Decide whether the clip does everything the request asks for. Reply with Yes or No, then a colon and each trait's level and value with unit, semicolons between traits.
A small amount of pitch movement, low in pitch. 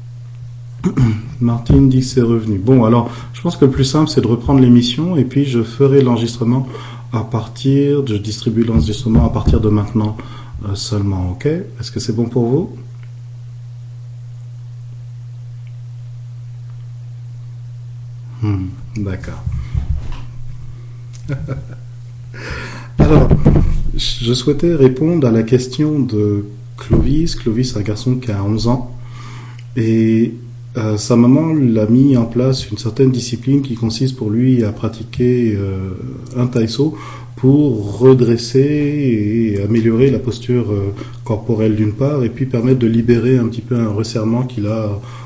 Yes: narrow, 1.9 semitones; low, 120 Hz